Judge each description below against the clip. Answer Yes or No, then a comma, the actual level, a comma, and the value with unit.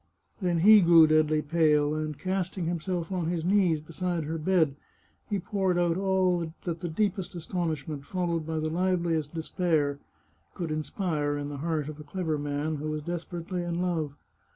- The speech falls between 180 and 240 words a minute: No, average, 170 wpm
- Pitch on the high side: No, medium, 165 Hz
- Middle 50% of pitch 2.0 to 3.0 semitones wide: Yes, average, 2.7 semitones